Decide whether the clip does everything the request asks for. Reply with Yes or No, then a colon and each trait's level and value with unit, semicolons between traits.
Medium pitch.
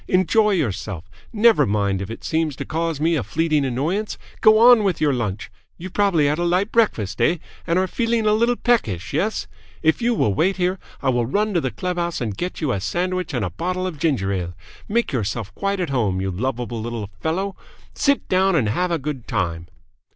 Yes: medium, 160 Hz